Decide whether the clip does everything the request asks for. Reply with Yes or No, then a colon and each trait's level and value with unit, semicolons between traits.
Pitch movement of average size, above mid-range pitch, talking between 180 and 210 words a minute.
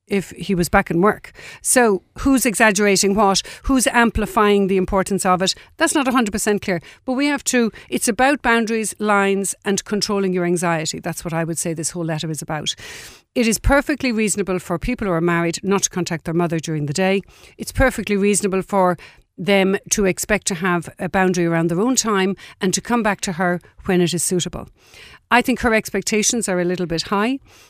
Yes: average, 3.8 semitones; high, 195 Hz; average, 200 wpm